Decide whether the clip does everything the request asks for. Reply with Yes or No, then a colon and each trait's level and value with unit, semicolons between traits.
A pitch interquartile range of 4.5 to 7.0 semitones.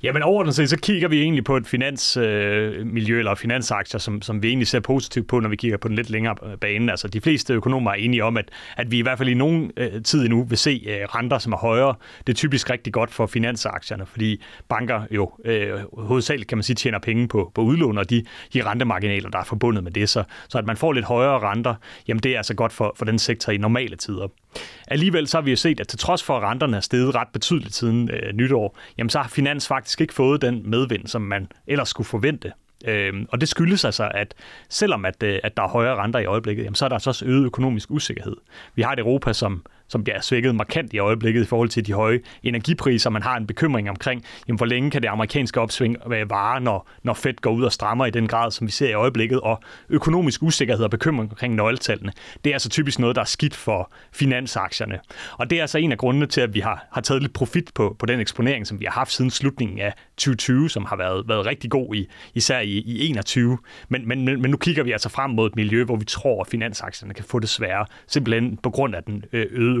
No: average, 3.4 semitones